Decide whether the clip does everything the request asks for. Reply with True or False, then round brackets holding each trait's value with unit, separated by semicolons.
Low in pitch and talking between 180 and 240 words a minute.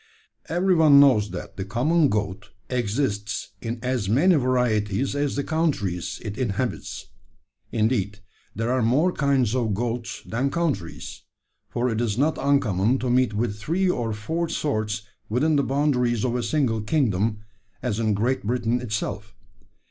False (120 Hz; 150 wpm)